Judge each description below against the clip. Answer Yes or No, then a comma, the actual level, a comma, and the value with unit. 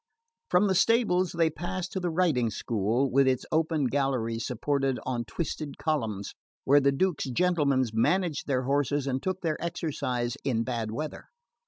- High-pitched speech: No, medium, 140 Hz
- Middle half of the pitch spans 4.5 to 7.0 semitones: Yes, average, 5.2 semitones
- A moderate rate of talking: Yes, average, 160 wpm